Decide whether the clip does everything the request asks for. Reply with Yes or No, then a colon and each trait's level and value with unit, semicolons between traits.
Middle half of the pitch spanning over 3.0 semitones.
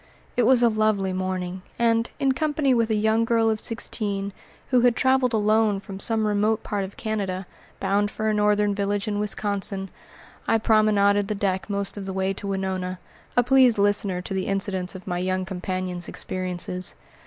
No: narrow, 2.5 semitones